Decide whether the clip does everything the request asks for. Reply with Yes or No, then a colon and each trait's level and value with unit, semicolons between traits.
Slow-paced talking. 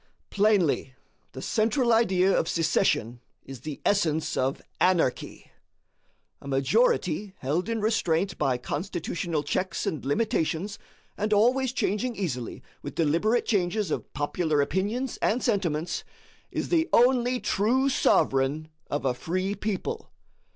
Yes: slow, 125 wpm